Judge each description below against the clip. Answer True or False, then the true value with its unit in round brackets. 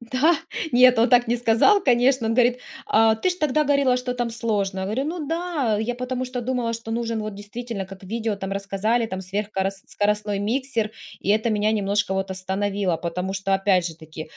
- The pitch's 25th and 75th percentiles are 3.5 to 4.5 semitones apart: True (4.0 semitones)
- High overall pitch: True (225 Hz)